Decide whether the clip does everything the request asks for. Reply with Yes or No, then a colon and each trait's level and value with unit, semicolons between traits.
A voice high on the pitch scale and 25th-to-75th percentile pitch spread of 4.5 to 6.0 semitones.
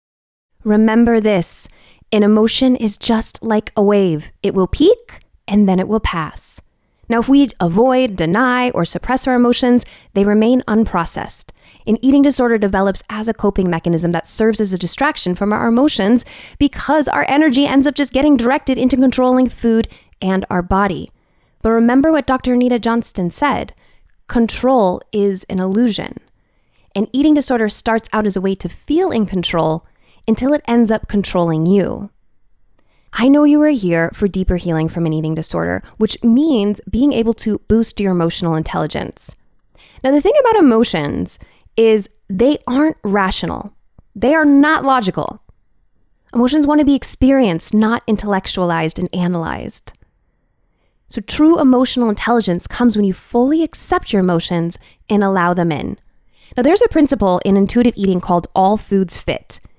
Yes: high, 220 Hz; average, 5.3 semitones